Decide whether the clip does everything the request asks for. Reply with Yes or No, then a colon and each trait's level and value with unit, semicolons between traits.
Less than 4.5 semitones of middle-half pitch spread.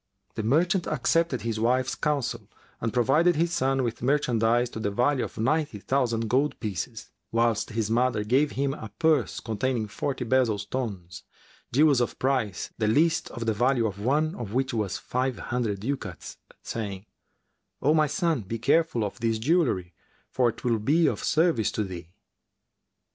Yes: average, 4.1 semitones